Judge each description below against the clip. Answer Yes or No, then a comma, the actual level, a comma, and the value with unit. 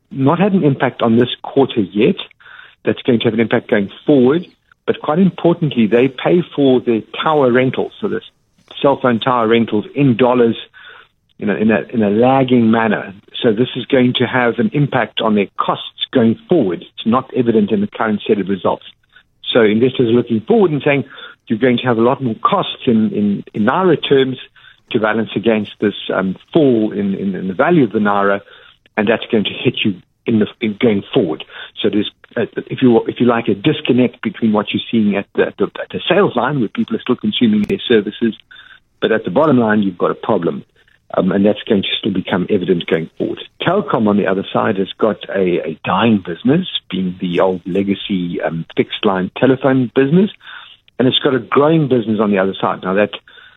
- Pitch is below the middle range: Yes, low, 120 Hz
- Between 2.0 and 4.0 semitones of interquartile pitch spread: No, average, 4.6 semitones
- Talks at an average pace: No, fast, 210 wpm